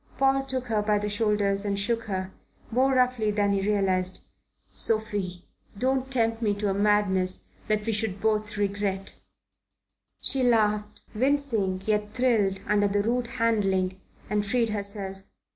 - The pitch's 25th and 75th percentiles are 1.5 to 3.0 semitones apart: Yes, narrow, 2.5 semitones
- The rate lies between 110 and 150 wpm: Yes, average, 145 wpm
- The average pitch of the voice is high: Yes, high, 210 Hz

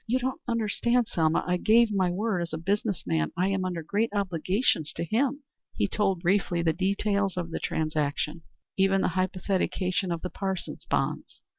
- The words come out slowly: No, average, 175 wpm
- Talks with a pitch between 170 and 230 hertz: Yes, high, 190 Hz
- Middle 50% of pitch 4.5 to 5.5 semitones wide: No, average, 3.5 semitones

